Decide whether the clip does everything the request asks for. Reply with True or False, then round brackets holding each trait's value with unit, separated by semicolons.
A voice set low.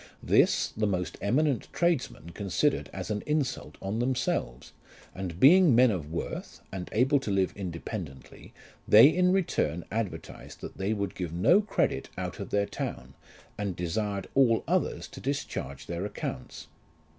True (105 Hz)